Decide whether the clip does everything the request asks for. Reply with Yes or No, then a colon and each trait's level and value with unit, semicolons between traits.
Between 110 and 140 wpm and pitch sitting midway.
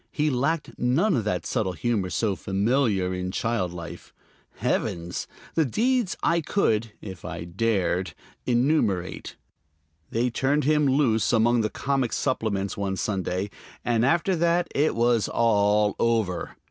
No: slow, 135 wpm; low, 115 Hz